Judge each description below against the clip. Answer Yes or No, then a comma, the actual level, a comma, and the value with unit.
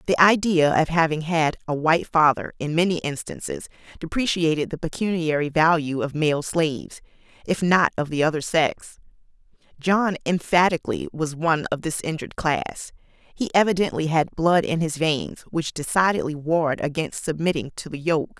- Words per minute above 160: No, average, 155 wpm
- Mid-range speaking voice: Yes, medium, 160 Hz